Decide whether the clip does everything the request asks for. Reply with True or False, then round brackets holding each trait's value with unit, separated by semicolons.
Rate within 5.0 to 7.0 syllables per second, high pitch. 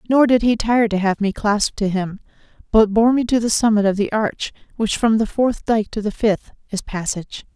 True (5.2 syllables/s; 215 Hz)